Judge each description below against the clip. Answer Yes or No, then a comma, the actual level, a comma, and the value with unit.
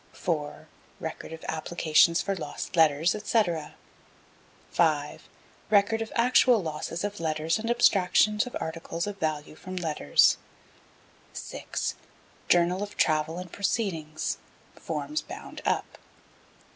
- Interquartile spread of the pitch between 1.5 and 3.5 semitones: No, average, 4.6 semitones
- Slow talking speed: Yes, slow, 115 wpm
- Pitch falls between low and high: Yes, medium, 175 Hz